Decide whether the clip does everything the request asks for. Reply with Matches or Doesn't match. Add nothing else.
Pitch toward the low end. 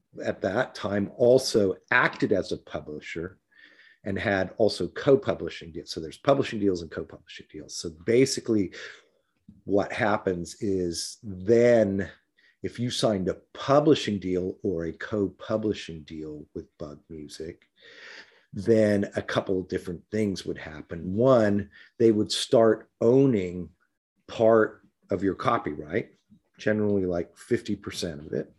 Matches